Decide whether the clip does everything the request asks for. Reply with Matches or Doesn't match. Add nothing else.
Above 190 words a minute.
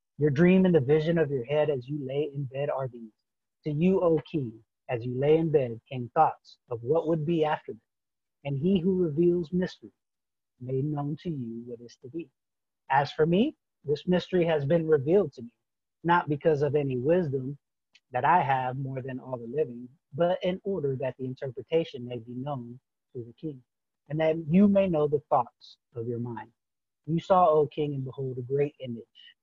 Matches